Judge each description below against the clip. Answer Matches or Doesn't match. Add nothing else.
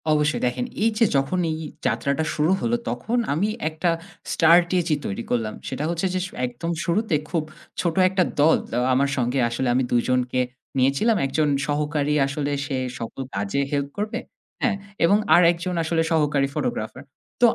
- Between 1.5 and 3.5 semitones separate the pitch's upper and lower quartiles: Doesn't match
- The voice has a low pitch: Doesn't match